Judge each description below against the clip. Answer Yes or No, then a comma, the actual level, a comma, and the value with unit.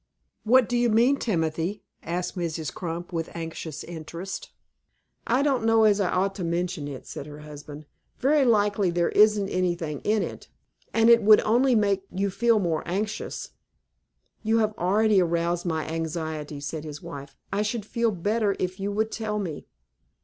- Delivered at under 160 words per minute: No, average, 170 wpm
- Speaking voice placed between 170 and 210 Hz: Yes, high, 190 Hz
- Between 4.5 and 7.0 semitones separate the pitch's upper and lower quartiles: Yes, average, 4.8 semitones